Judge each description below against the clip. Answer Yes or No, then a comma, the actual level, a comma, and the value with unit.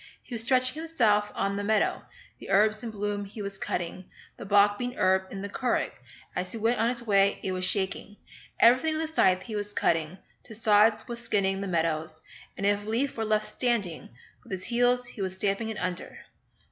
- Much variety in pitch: No, average, 3.3 semitones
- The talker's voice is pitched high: Yes, high, 205 Hz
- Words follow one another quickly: Yes, fast, 210 wpm